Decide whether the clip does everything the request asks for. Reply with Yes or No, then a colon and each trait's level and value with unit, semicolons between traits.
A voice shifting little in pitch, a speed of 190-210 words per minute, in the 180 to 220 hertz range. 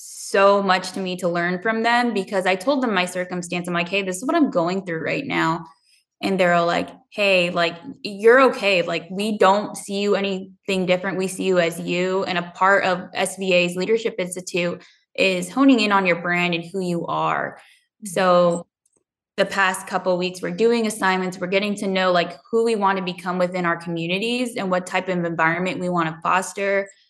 Yes: narrow, 2.0 semitones; fast, 205 wpm; medium, 185 Hz